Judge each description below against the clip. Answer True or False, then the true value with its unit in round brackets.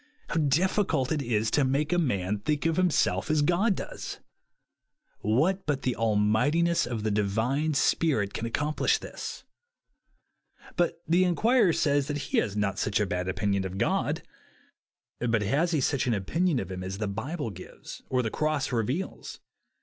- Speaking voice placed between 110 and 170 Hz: True (135 Hz)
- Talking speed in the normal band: True (165 wpm)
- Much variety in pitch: True (7.4 semitones)